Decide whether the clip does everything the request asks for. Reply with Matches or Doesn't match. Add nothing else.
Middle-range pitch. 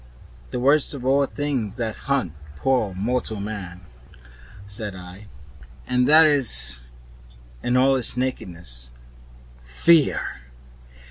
Doesn't match